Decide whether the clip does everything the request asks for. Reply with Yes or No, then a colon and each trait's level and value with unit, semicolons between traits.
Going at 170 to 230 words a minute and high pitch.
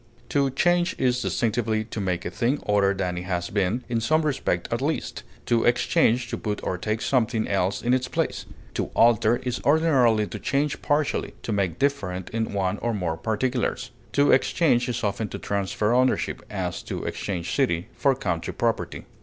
No: average, 180 wpm; low, 115 Hz